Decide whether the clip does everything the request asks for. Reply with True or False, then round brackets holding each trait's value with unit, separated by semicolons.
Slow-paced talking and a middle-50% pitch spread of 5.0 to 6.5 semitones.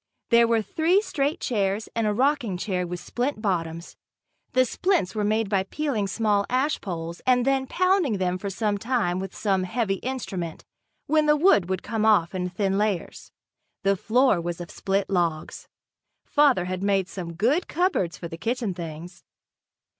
False (170 wpm; 5.6 semitones)